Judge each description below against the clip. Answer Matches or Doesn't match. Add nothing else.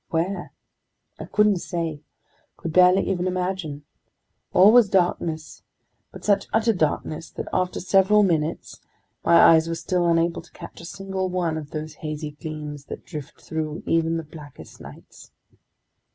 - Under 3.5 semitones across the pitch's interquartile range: Matches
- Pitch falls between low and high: Matches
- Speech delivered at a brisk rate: Doesn't match